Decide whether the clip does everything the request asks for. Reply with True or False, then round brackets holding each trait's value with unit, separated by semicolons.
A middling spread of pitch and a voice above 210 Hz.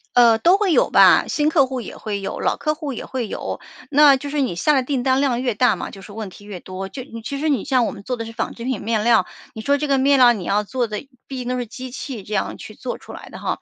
True (4.1 semitones; 250 Hz)